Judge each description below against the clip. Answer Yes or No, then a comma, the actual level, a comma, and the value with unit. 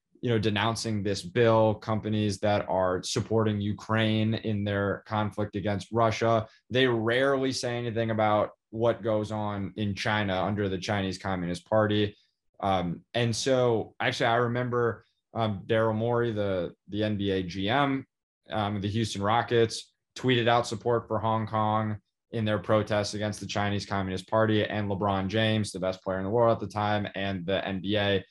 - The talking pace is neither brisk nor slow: Yes, average, 160 wpm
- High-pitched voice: No, low, 105 Hz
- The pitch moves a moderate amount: No, narrow, 2.2 semitones